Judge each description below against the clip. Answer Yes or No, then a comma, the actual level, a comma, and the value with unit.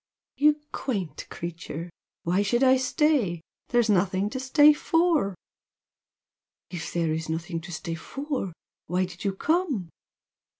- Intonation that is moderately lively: No, wide, 8.0 semitones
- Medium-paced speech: No, slow, 125 wpm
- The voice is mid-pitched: No, high, 195 Hz